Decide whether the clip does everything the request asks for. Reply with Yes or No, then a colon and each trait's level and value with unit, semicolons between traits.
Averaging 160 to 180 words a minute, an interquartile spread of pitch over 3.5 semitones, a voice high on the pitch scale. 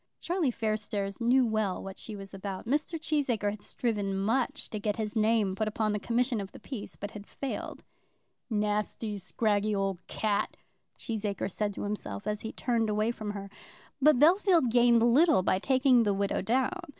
No: average, 175 wpm; average, 3.2 semitones; high, 215 Hz